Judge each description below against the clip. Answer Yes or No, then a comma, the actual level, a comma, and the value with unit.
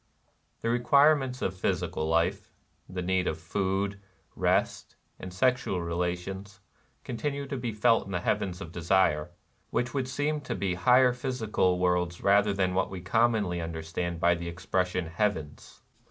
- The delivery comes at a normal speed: Yes, average, 165 wpm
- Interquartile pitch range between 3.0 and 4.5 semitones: No, average, 5.2 semitones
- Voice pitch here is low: Yes, very low, 95 Hz